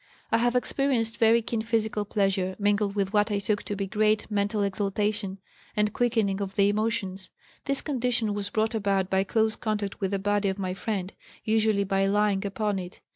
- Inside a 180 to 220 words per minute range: Yes, average, 185 wpm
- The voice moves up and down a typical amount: No, narrow, 1.9 semitones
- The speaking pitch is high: Yes, high, 205 Hz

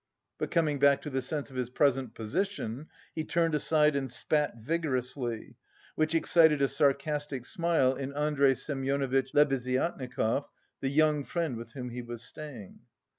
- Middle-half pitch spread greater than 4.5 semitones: No, average, 3.0 semitones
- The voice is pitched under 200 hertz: Yes, medium, 140 Hz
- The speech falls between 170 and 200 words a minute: No, average, 150 wpm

